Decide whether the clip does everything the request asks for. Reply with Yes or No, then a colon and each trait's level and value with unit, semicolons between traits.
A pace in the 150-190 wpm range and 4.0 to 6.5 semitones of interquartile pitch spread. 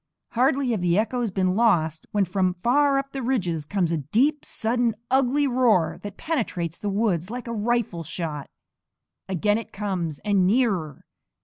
Yes: average, 165 wpm; wide, 5.6 semitones